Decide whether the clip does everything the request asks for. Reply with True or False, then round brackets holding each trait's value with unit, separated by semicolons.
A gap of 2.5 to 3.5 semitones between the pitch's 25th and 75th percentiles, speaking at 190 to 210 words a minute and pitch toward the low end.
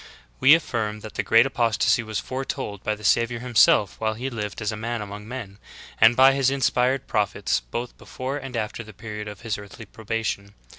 True (2.9 semitones; 205 wpm; 115 Hz)